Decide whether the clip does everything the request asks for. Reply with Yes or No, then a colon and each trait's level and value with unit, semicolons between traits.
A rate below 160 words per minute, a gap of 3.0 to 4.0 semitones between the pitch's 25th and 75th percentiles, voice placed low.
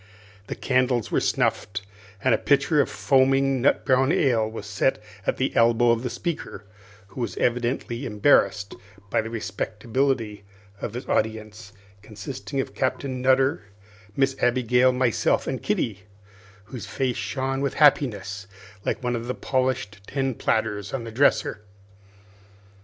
Yes: average, 140 wpm; average, 3.5 semitones; low, 125 Hz